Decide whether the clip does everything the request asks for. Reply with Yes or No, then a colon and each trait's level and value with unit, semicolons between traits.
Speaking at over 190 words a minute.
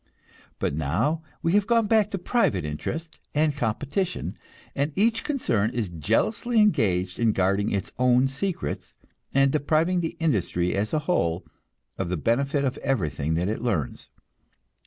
No: average, 145 wpm